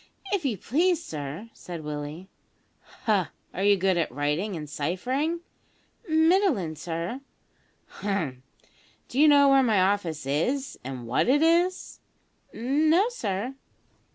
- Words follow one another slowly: Yes, slow, 125 wpm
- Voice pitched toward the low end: No, high, 205 Hz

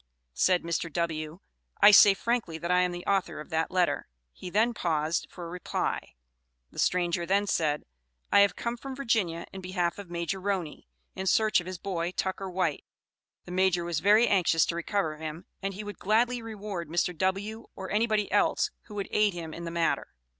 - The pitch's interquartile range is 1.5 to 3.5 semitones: Yes, average, 3.1 semitones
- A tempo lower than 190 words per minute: No, average, 195 wpm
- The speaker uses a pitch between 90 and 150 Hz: No, medium, 185 Hz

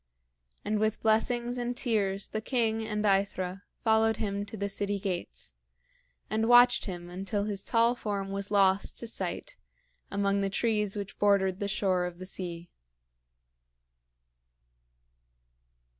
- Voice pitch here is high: Yes, high, 205 Hz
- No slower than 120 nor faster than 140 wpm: Yes, slow, 135 wpm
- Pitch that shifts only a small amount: Yes, narrow, 2.3 semitones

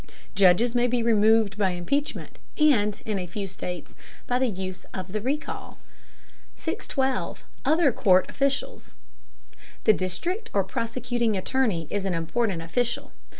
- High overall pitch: Yes, high, 215 Hz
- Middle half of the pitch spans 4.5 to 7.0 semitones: Yes, average, 4.9 semitones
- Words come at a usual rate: No, slow, 130 wpm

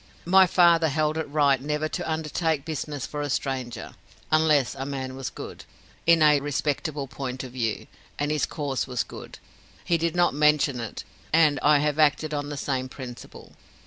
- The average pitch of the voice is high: No, medium, 145 Hz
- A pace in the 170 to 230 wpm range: Yes, average, 175 wpm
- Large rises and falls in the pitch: No, average, 2.7 semitones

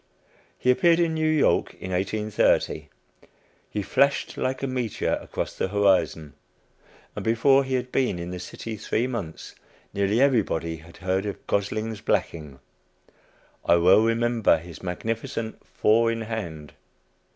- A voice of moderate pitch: No, low, 110 Hz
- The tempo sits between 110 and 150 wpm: Yes, average, 140 wpm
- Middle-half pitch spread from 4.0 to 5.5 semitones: Yes, average, 5.0 semitones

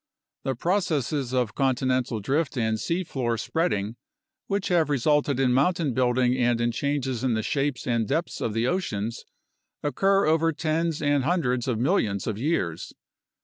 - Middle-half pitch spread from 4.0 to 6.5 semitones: Yes, average, 5.0 semitones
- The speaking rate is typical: Yes, average, 155 wpm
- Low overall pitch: Yes, low, 130 Hz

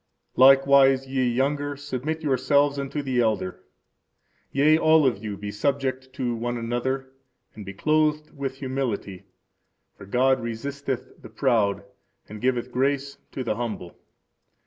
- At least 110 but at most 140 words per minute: Yes, slow, 135 wpm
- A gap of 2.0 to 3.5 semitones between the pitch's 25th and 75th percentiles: Yes, average, 2.9 semitones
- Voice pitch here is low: Yes, low, 130 Hz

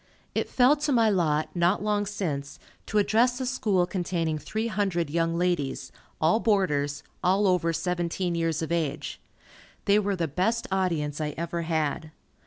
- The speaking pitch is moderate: Yes, medium, 175 Hz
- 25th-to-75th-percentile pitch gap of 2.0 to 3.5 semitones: No, average, 4.4 semitones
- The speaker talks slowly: No, average, 160 wpm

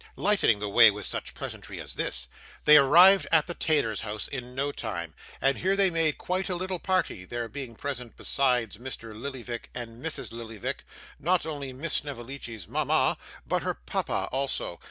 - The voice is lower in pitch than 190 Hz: Yes, low, 135 Hz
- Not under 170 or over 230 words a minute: Yes, average, 175 wpm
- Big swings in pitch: Yes, wide, 5.7 semitones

